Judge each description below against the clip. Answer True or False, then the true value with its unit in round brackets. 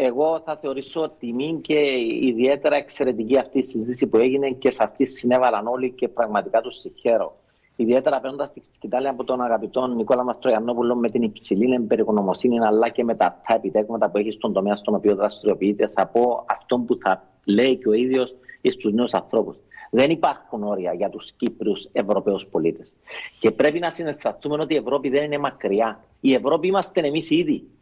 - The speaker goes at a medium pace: False (175 wpm)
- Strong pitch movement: False (3.8 semitones)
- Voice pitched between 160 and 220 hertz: False (125 Hz)